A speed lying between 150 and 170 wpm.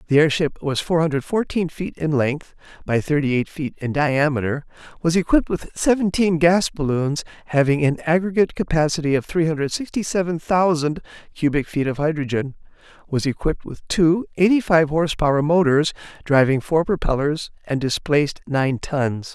Yes: average, 160 wpm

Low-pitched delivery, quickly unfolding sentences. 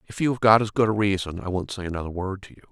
Yes: low, 100 Hz; fast, 330 wpm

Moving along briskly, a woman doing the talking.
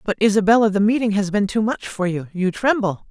Yes: fast, 230 wpm; female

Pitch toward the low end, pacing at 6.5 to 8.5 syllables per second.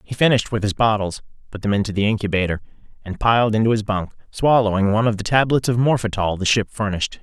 Yes: low, 105 Hz; 6.7 syllables/s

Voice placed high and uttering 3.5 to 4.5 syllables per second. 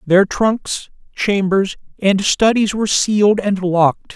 Yes: high, 200 Hz; 3.9 syllables/s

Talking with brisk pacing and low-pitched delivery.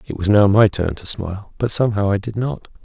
Yes: fast, 255 wpm; low, 100 Hz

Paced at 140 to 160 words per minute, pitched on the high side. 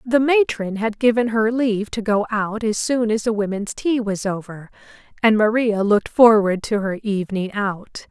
No: average, 185 wpm; high, 215 Hz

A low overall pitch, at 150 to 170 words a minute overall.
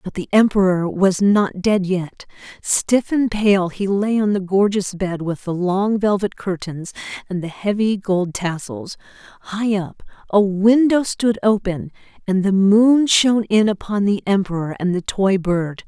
No: high, 195 Hz; average, 165 wpm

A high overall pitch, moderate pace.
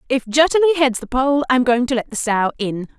No: very high, 260 Hz; fast, 240 wpm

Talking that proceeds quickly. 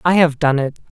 Yes: fast, 240 wpm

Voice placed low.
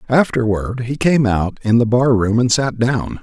Yes: low, 120 Hz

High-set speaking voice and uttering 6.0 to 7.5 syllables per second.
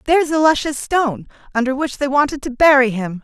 Yes: very high, 275 Hz; 6.1 syllables/s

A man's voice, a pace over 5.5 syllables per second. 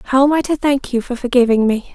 No: female; 5.8 syllables/s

